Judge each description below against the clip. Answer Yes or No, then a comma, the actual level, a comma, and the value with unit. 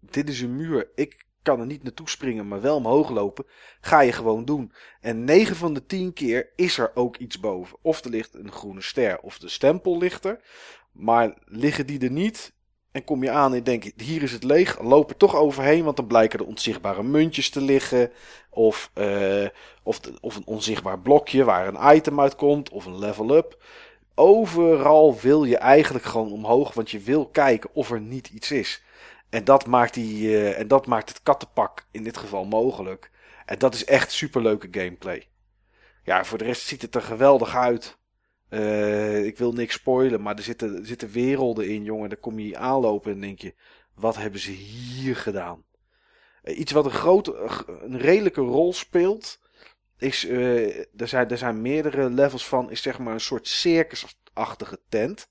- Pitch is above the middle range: No, low, 125 Hz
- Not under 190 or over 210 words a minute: Yes, average, 195 wpm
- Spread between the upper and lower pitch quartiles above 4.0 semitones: Yes, average, 4.8 semitones